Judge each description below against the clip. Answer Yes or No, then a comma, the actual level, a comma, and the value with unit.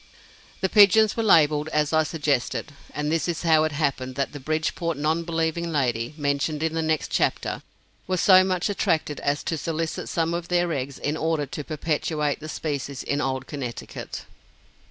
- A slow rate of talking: No, average, 175 wpm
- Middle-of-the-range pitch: Yes, medium, 155 Hz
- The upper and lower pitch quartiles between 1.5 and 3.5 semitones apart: Yes, narrow, 2.4 semitones